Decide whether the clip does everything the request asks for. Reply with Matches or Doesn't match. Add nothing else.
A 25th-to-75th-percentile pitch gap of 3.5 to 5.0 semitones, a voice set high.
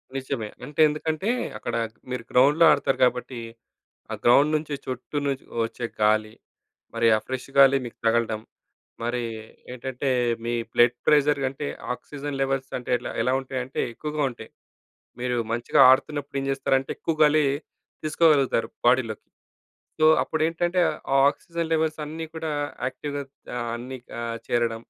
Doesn't match